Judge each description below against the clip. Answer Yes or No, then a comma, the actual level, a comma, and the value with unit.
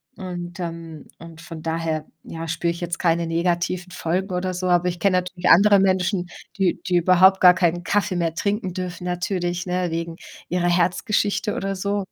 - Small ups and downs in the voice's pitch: Yes, narrow, 1.7 semitones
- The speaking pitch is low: No, medium, 180 Hz